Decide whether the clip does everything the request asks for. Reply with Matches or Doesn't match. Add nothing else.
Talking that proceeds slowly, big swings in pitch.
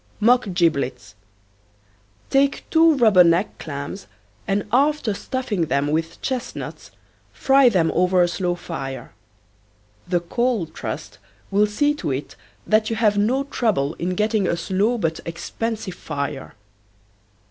Matches